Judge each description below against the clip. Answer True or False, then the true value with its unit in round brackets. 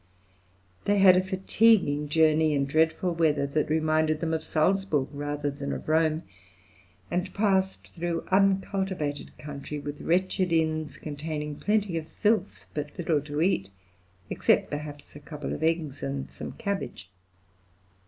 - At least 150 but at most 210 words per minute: False (140 wpm)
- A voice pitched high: False (155 Hz)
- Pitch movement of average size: True (4.0 semitones)